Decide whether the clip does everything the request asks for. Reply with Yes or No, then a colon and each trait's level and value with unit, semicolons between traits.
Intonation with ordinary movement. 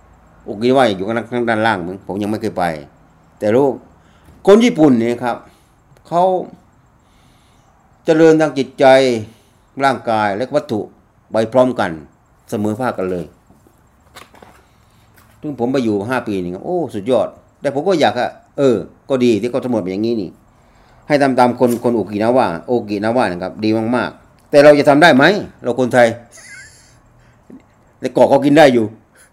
Yes: average, 3.7 semitones